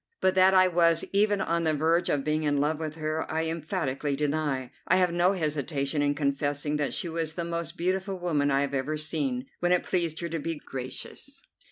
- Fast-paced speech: Yes, fast, 210 wpm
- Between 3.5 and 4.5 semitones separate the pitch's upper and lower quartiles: No, average, 3.0 semitones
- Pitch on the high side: No, medium, 155 Hz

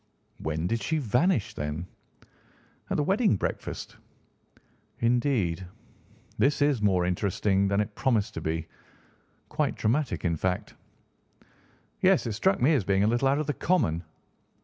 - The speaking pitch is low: Yes, low, 110 Hz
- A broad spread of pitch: Yes, wide, 7.5 semitones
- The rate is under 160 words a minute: Yes, average, 145 wpm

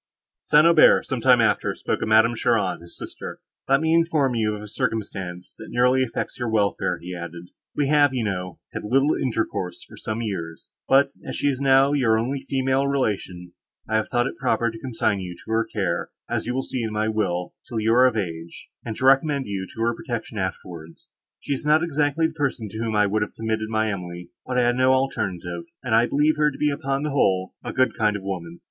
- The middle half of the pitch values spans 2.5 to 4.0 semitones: No, average, 5.2 semitones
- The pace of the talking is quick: Yes, fast, 225 wpm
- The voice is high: No, low, 115 Hz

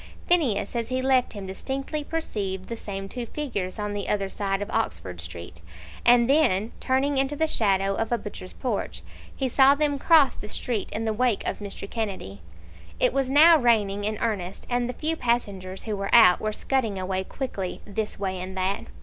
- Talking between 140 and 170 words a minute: No, average, 190 wpm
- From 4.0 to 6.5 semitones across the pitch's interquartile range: Yes, average, 5.0 semitones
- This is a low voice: No, high, 220 Hz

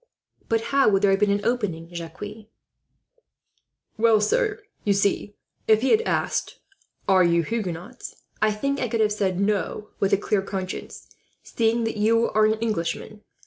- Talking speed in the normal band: Yes, average, 165 wpm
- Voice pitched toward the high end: Yes, high, 210 Hz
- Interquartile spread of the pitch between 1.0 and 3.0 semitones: Yes, average, 2.7 semitones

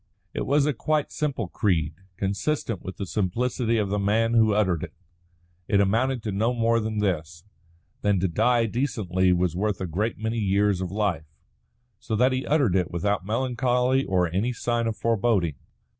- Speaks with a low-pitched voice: Yes, low, 105 Hz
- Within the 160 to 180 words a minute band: Yes, average, 175 wpm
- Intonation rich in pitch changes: No, average, 3.9 semitones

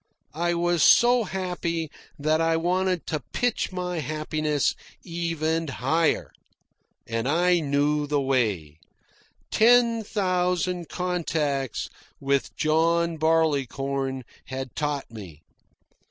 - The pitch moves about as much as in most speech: Yes, average, 4.1 semitones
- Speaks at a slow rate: Yes, slow, 100 wpm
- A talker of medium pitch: Yes, medium, 160 Hz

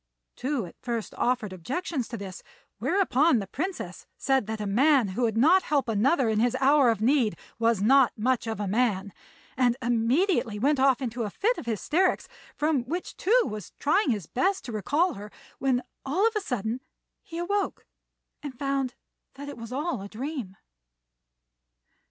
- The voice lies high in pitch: Yes, very high, 250 Hz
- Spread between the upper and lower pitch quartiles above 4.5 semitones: Yes, average, 5.0 semitones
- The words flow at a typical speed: Yes, average, 175 wpm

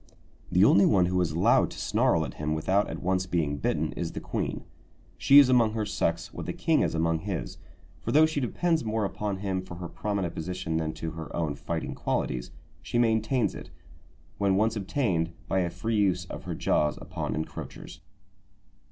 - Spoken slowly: No, average, 195 wpm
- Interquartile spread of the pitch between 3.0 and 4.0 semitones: No, average, 4.7 semitones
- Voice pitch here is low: Yes, very low, 95 Hz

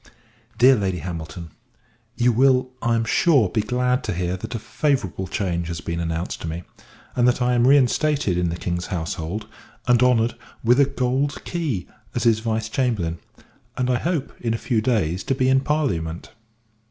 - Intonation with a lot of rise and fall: Yes, wide, 6.3 semitones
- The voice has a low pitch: Yes, low, 115 Hz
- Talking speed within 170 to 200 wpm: Yes, average, 180 wpm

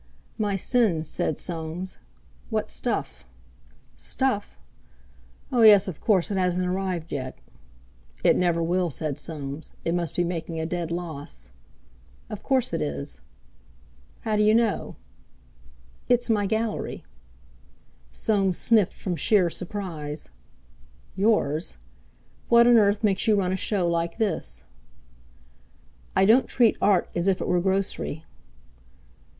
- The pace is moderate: No, slow, 125 wpm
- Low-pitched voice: No, medium, 185 Hz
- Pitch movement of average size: Yes, average, 4.2 semitones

